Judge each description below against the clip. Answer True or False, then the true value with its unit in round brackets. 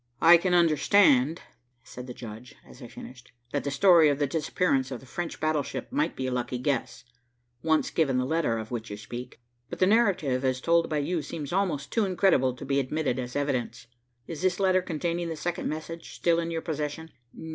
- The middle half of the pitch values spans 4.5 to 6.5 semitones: True (4.8 semitones)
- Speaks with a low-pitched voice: False (150 Hz)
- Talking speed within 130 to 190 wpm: False (200 wpm)